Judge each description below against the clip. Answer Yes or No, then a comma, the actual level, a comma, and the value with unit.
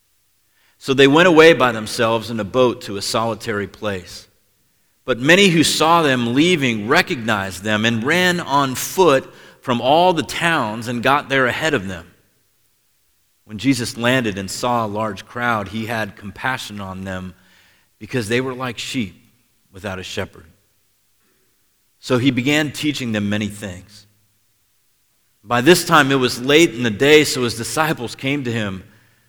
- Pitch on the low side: Yes, low, 115 Hz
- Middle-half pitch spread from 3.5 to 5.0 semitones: Yes, average, 3.8 semitones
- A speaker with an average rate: Yes, average, 160 wpm